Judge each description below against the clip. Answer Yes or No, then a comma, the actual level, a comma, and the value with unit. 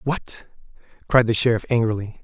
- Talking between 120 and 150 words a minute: Yes, slow, 135 wpm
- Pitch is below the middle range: Yes, low, 115 Hz